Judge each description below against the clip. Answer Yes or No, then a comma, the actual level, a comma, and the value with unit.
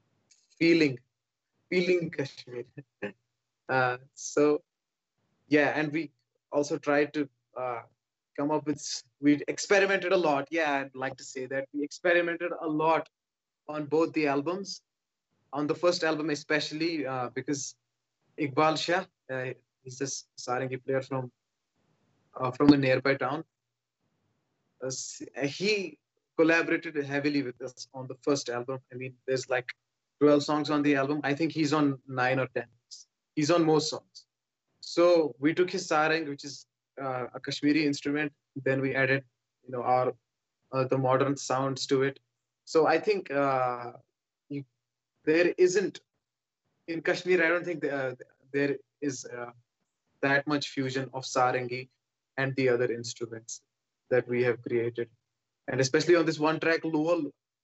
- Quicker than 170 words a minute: No, average, 150 wpm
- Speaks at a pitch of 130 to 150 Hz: Yes, medium, 140 Hz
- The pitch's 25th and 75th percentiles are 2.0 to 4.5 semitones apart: Yes, average, 3.4 semitones